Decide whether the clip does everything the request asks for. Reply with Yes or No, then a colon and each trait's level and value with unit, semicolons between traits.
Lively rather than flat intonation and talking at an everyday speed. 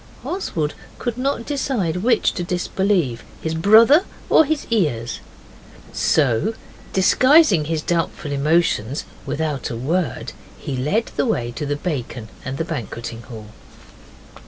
No: wide, 8.6 semitones; slow, 130 wpm